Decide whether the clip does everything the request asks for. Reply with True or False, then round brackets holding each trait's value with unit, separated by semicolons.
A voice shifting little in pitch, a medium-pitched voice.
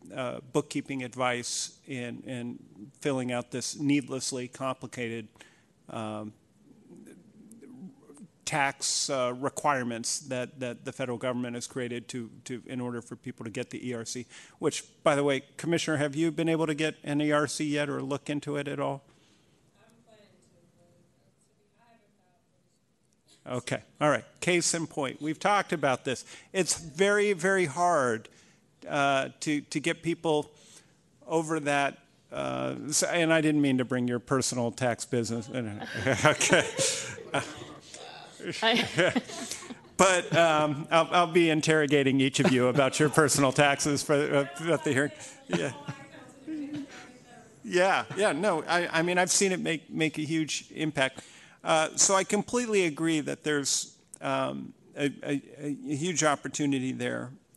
False (4.3 semitones; 145 Hz)